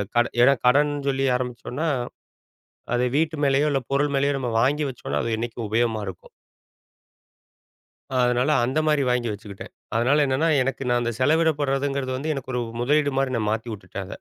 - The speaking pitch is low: Yes, low, 130 Hz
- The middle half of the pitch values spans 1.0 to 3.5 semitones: Yes, average, 3.1 semitones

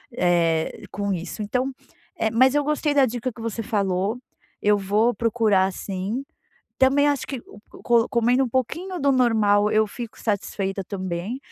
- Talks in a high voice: Yes, high, 225 Hz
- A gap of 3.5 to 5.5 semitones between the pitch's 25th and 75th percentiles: Yes, average, 4.4 semitones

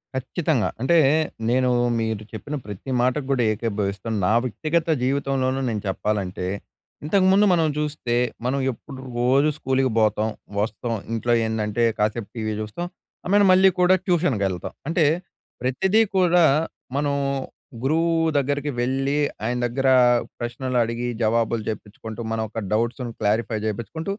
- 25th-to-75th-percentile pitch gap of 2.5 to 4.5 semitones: No, average, 5.2 semitones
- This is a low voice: Yes, low, 125 Hz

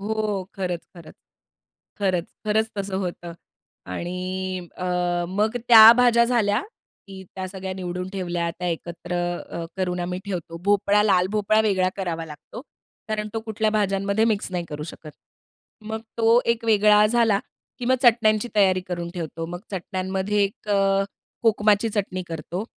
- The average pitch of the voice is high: Yes, high, 195 Hz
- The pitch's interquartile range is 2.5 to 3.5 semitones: Yes, average, 3.1 semitones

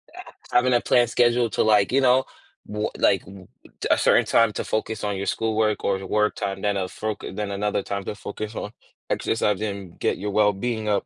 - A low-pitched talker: Yes, low, 105 Hz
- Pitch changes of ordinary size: No, narrow, 2.1 semitones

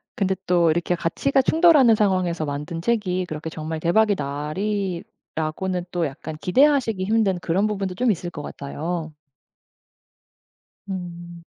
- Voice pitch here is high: No, medium, 180 Hz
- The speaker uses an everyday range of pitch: Yes, average, 4.1 semitones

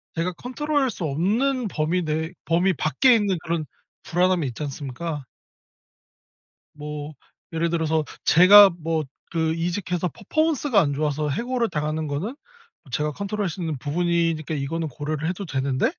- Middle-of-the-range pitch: Yes, medium, 165 Hz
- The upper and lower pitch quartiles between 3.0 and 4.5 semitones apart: Yes, average, 4.1 semitones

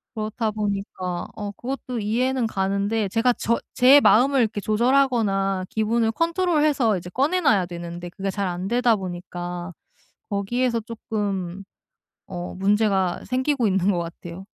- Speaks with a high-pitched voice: Yes, high, 210 Hz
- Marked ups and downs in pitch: No, average, 4.4 semitones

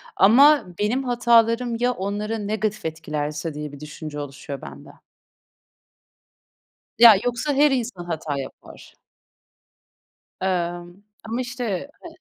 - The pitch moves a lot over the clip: Yes, wide, 7.2 semitones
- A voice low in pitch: No, high, 210 Hz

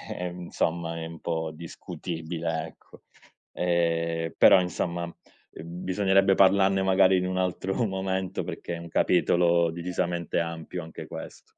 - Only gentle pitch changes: Yes, narrow, 2.0 semitones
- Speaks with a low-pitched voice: Yes, very low, 85 Hz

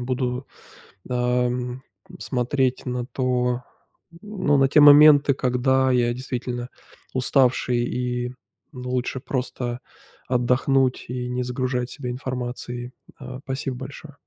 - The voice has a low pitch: Yes, low, 125 Hz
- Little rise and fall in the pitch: Yes, narrow, 1.2 semitones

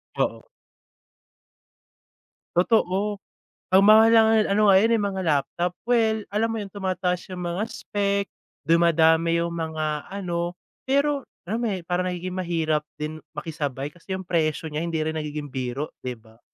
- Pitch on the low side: No, medium, 175 Hz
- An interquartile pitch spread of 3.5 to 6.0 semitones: Yes, average, 4.2 semitones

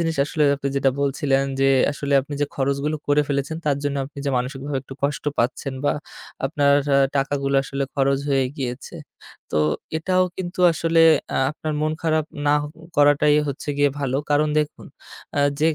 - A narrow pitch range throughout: Yes, narrow, 1.6 semitones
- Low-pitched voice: No, medium, 145 Hz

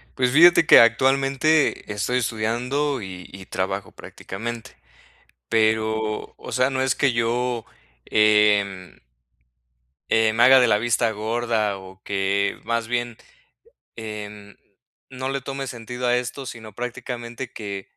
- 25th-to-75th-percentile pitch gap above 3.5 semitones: No, average, 3.0 semitones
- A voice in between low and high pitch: No, low, 115 Hz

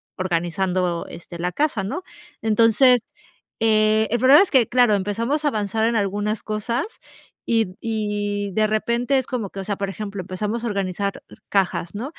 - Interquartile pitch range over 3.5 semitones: No, average, 3.0 semitones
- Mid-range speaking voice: No, high, 215 Hz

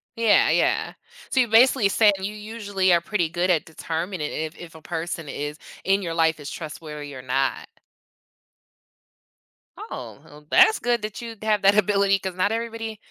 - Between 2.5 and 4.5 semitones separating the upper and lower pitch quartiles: No, average, 4.9 semitones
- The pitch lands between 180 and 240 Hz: Yes, high, 190 Hz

